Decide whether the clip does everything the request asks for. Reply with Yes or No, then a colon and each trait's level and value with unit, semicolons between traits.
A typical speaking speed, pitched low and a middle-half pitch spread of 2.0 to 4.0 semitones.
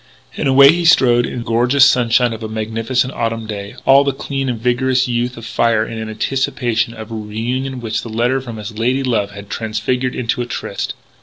No: fast, 210 wpm; low, 120 Hz; average, 2.7 semitones